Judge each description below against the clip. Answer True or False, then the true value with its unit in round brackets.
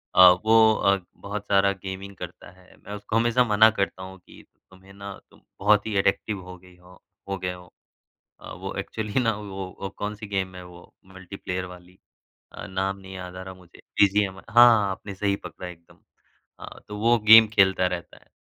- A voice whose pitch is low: True (95 Hz)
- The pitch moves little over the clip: True (2.1 semitones)